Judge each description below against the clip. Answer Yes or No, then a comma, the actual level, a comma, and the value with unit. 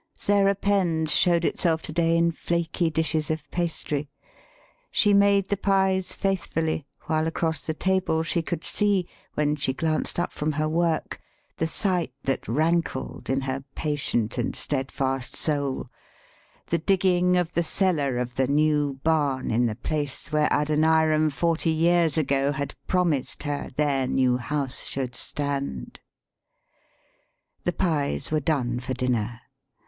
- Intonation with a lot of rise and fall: No, average, 3.7 semitones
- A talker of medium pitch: Yes, medium, 155 Hz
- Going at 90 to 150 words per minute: Yes, average, 145 wpm